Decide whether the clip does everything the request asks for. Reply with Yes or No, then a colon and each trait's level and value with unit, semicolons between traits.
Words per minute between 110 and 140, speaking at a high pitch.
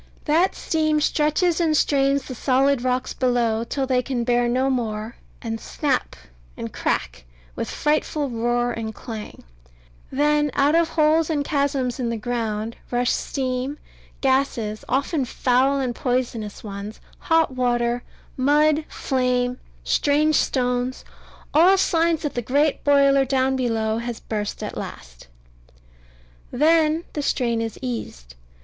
Yes: slow, 135 wpm; very high, 255 Hz